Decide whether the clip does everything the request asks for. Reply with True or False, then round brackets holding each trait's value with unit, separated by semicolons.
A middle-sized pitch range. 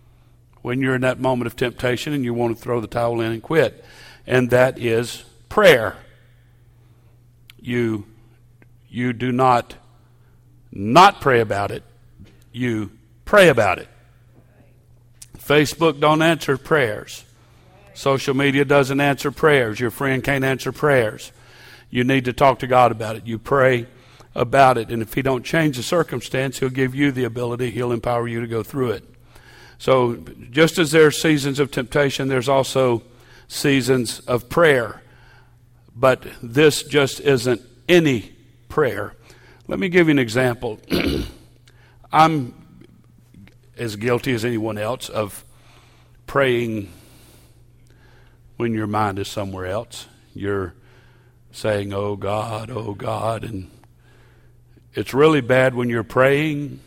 False (1.9 semitones)